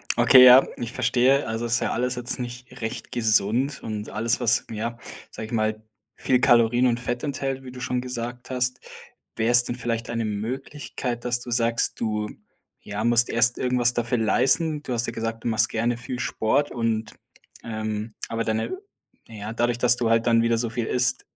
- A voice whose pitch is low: Yes, low, 120 Hz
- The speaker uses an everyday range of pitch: No, narrow, 1.8 semitones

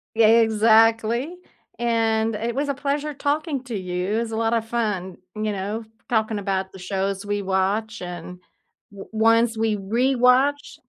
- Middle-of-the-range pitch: No, high, 225 Hz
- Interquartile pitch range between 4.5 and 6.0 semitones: No, average, 3.0 semitones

